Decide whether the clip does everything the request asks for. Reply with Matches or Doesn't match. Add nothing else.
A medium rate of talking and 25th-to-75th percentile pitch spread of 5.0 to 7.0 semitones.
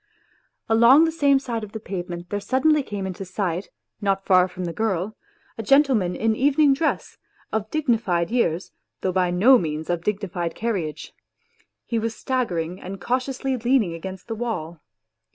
Matches